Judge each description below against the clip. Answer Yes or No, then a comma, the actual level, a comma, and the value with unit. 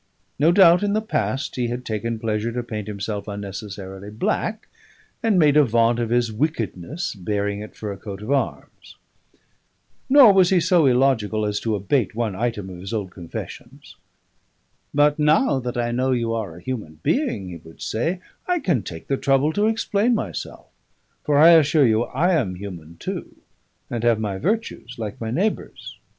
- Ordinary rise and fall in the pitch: No, wide, 6.8 semitones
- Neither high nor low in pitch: No, low, 120 Hz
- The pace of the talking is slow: No, average, 180 wpm